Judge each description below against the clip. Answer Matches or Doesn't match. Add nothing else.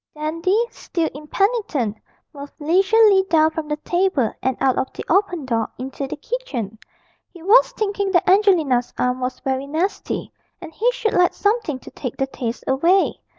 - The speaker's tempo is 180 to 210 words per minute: Doesn't match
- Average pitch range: Doesn't match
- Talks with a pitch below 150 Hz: Doesn't match